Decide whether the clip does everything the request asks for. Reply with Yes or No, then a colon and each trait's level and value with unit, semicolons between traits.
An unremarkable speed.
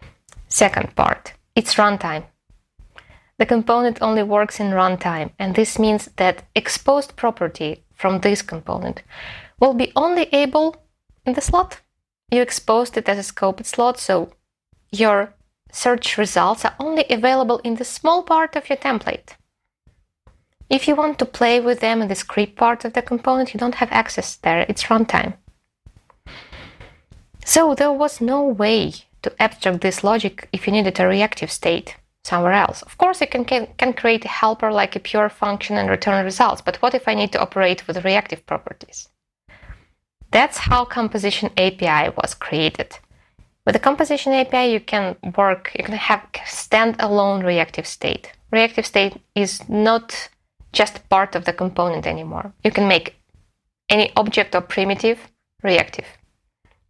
Yes: average, 155 wpm